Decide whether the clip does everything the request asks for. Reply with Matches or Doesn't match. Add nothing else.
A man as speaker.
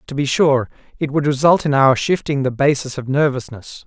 Matches